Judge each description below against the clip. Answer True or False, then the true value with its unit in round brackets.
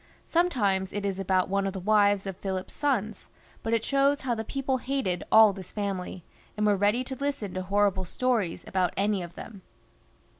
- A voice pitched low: False (205 Hz)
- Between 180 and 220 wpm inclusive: True (190 wpm)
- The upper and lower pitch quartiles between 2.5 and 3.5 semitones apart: False (4.1 semitones)